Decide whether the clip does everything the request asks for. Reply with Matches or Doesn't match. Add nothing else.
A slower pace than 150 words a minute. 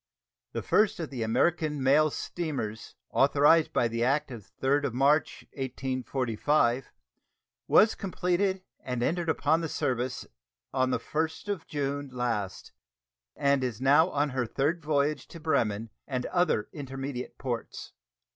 Matches